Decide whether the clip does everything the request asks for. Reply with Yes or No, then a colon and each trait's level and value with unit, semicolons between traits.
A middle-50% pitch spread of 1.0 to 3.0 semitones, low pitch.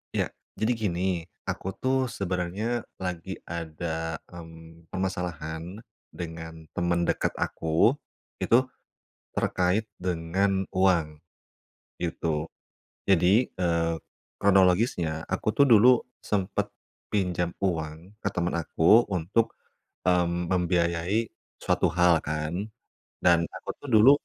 Yes: narrow, 2.4 semitones; very low, 90 Hz